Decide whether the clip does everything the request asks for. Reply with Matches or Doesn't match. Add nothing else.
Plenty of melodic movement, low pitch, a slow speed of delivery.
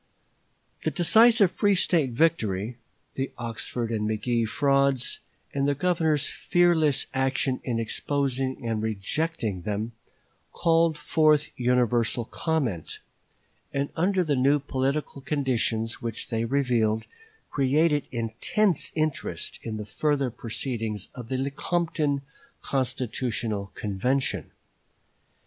Doesn't match